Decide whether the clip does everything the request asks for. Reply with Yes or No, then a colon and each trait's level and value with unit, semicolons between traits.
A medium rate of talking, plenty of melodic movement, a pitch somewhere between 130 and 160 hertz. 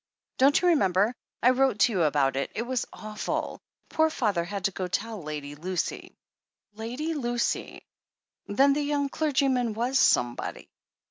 No: average, 155 wpm; wide, 6.5 semitones; high, 230 Hz